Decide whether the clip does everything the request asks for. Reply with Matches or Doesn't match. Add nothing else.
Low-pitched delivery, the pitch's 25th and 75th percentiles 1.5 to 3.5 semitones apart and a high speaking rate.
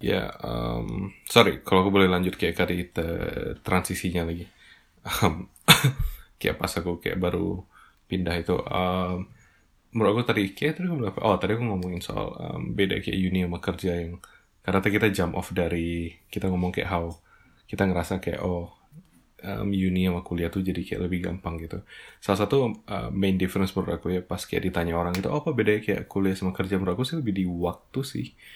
Matches